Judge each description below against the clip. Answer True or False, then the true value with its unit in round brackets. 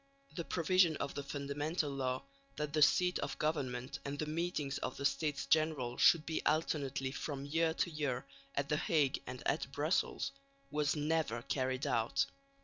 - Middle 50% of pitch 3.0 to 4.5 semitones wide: False (2.5 semitones)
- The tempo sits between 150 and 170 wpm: True (165 wpm)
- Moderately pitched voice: True (145 Hz)